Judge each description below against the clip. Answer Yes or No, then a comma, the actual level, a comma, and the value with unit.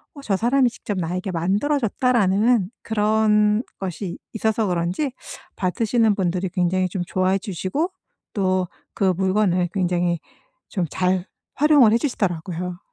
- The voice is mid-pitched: No, high, 195 Hz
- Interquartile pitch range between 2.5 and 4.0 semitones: Yes, average, 3.4 semitones